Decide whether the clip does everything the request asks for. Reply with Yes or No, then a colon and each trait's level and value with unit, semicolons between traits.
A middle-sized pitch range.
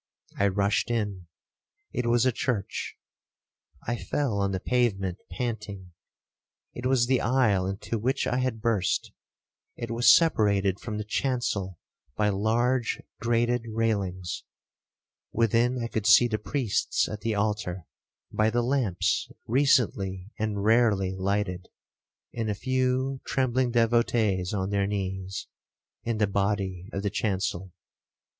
Yes: average, 3.5 semitones